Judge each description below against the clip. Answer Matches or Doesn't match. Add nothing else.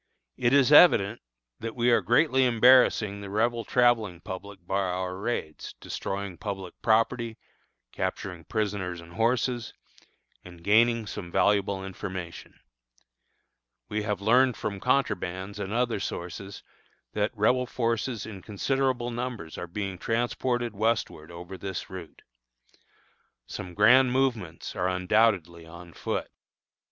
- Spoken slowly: Matches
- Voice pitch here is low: Matches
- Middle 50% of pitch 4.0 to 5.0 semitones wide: Matches